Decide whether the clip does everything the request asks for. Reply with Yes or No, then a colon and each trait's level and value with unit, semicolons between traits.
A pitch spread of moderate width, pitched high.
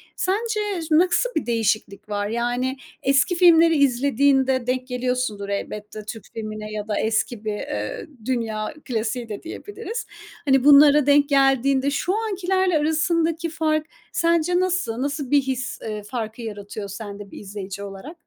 No: wide, 6.7 semitones; very high, 260 Hz